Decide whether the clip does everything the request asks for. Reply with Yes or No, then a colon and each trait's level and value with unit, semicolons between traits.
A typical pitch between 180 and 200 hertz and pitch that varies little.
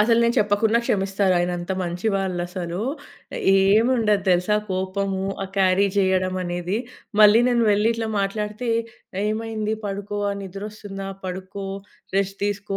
Yes: high, 195 Hz; narrow, 2.1 semitones